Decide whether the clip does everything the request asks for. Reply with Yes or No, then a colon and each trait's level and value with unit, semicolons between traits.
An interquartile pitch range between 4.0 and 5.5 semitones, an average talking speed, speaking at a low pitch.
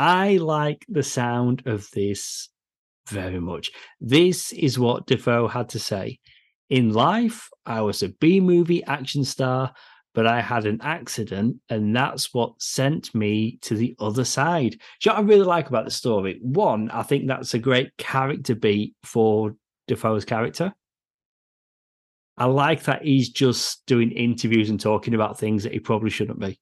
Yes: average, 4.3 semitones; average, 170 wpm; low, 120 Hz